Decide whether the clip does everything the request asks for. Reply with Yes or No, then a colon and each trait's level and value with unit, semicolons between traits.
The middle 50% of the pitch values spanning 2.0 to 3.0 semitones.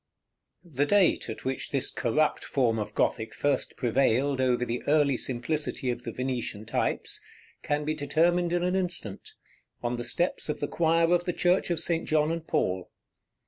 No: average, 5.3 semitones